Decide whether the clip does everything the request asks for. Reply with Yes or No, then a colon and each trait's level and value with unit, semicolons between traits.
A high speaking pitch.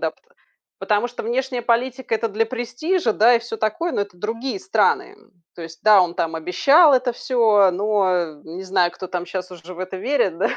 Yes: high, 215 Hz